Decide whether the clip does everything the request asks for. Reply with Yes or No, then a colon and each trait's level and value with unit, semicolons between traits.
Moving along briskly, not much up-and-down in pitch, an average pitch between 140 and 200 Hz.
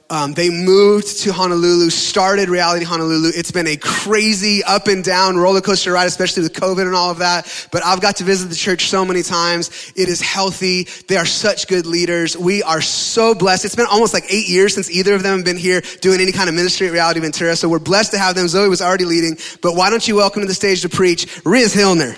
Yes: fast, 245 wpm; narrow, 2.2 semitones; medium, 185 Hz